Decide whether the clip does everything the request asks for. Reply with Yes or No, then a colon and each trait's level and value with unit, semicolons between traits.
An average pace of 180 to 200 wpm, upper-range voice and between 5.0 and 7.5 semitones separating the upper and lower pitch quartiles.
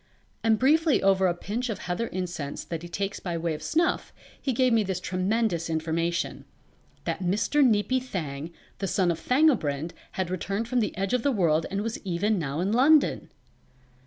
Yes: average, 185 wpm; high, 195 Hz; average, 5.3 semitones